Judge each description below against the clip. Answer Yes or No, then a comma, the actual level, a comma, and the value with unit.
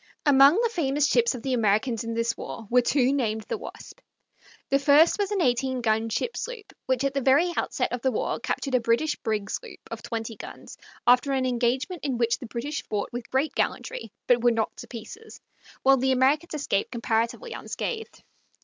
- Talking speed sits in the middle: Yes, average, 195 wpm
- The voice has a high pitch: Yes, very high, 260 Hz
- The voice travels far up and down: No, average, 3.9 semitones